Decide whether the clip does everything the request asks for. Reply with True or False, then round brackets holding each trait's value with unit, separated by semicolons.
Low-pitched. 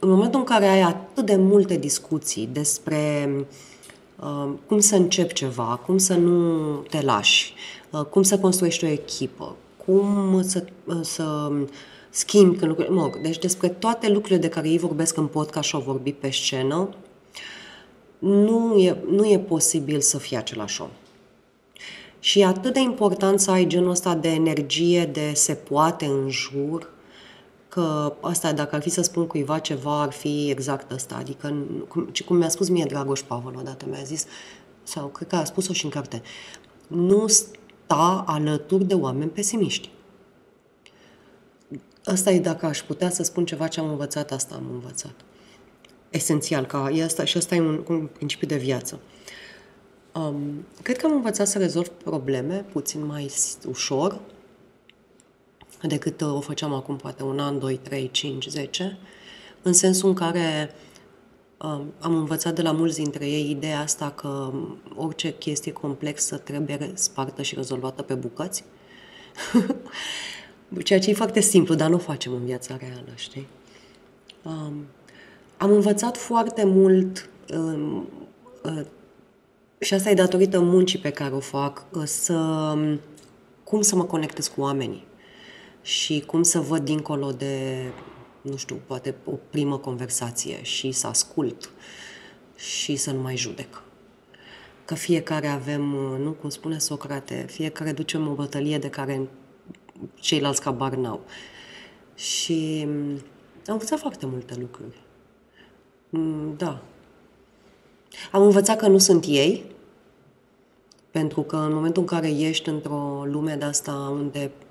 False (155 Hz)